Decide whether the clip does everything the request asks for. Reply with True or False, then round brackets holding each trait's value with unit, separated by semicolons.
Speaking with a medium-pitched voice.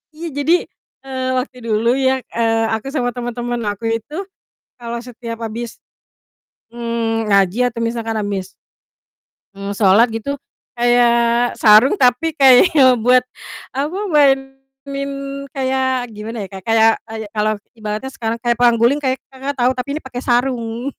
False (240 Hz)